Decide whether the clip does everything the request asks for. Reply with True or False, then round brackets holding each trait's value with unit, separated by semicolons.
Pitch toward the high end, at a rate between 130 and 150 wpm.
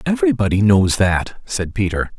False (105 Hz; 135 wpm)